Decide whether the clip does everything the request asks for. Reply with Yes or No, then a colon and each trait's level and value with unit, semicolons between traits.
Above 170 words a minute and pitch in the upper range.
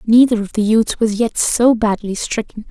Yes: average, 200 wpm; high, 225 Hz